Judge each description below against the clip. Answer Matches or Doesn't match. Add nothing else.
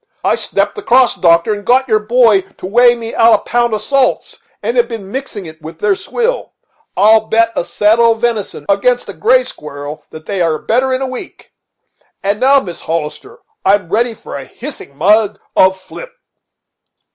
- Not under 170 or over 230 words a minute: Matches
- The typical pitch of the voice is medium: Doesn't match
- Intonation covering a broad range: Doesn't match